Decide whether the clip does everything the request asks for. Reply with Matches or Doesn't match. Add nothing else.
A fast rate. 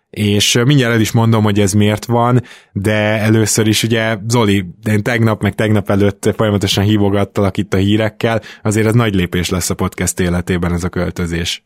Matches